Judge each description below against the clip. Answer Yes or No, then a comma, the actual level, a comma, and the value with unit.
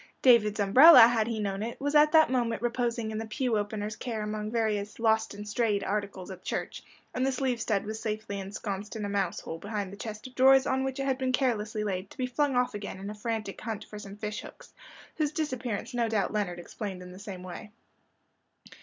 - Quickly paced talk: Yes, fast, 225 wpm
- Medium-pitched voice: No, high, 220 Hz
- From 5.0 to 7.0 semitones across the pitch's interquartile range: No, average, 3.3 semitones